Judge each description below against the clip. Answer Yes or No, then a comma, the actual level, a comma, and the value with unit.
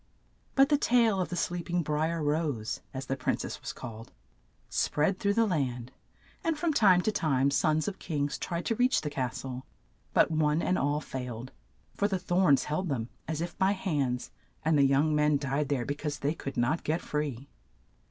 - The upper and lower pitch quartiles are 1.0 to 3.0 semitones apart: No, average, 4.7 semitones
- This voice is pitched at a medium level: Yes, medium, 150 Hz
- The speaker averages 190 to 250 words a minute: Yes, average, 200 wpm